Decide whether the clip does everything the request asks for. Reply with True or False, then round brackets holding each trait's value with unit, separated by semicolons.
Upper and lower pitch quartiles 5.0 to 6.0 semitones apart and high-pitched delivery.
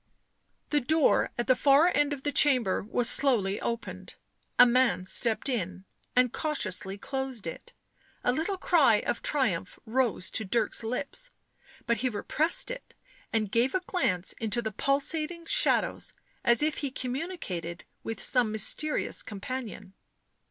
True (5.3 semitones; 250 Hz)